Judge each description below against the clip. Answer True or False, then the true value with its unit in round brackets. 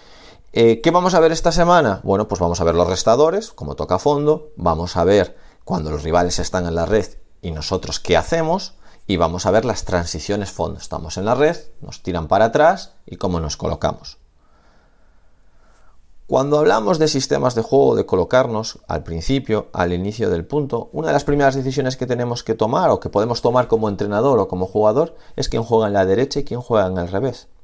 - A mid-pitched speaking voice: False (110 Hz)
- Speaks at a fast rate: True (205 wpm)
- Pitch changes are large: True (7.6 semitones)